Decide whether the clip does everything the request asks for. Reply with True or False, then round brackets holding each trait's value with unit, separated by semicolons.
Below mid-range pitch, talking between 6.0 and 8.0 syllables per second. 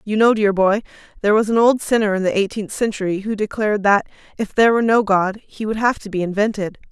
False (210 Hz; 6.4 syllables/s)